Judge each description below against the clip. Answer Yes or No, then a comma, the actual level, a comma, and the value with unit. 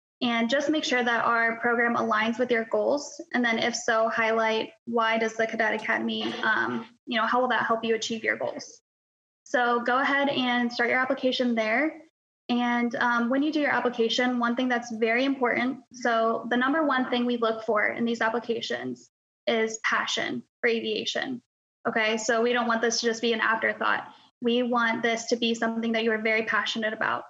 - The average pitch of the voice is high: Yes, high, 235 Hz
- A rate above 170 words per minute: Yes, average, 200 wpm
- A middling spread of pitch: No, narrow, 1.7 semitones